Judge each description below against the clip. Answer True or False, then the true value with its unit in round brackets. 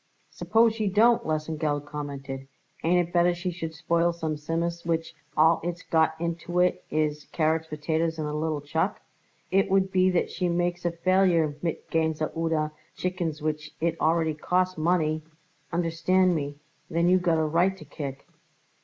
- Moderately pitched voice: True (165 Hz)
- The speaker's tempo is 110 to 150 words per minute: False (170 wpm)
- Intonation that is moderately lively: False (2.2 semitones)